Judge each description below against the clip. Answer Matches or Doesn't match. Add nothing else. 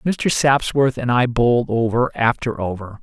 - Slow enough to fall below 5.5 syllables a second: Matches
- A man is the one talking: Matches